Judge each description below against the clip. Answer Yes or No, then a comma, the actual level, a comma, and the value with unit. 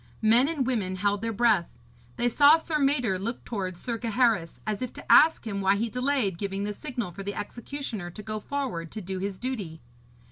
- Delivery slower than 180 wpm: No, fast, 205 wpm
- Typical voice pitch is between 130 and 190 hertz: No, high, 220 Hz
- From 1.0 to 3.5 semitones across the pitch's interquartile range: No, average, 4.3 semitones